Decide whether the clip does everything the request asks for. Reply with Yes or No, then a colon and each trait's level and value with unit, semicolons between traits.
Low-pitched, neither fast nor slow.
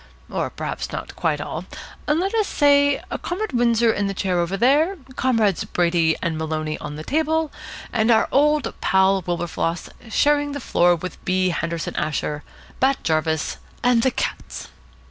No: high, 195 Hz; average, 155 wpm